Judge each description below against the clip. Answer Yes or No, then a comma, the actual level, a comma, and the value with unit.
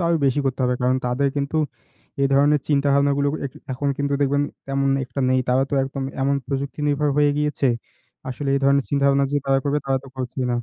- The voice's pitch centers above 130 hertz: Yes, medium, 140 Hz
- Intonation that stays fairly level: Yes, narrow, 1.0 semitones